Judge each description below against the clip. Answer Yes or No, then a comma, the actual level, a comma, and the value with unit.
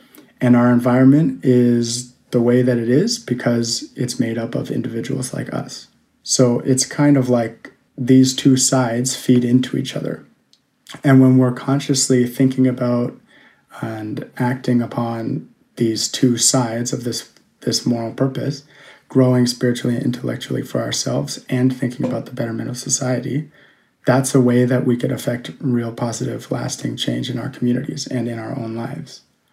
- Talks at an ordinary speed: Yes, average, 160 wpm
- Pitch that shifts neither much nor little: No, narrow, 1.7 semitones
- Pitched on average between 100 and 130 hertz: Yes, low, 125 Hz